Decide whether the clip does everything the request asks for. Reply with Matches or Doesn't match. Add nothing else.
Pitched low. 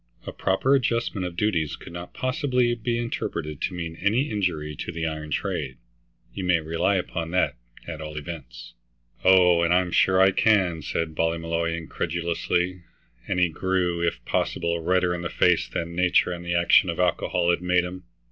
Matches